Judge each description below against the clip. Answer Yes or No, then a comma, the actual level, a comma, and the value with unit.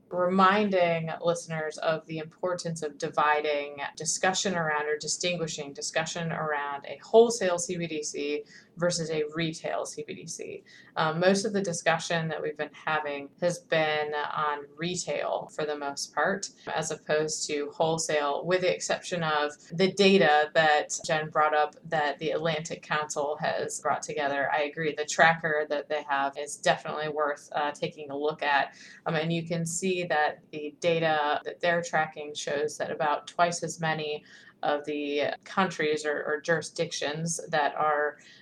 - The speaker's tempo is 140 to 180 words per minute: Yes, average, 155 wpm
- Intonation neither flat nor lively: No, narrow, 2.3 semitones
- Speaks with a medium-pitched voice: Yes, medium, 155 Hz